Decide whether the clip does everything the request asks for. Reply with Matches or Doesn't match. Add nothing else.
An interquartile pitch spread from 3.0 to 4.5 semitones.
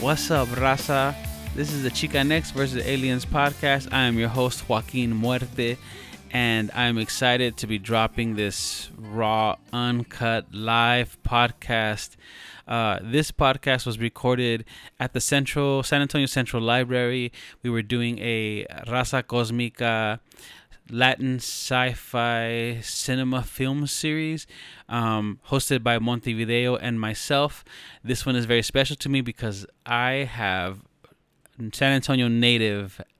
Doesn't match